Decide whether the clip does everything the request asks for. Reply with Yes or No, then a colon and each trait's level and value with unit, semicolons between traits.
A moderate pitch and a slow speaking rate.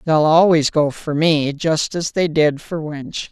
No: medium, 155 Hz; average, 200 wpm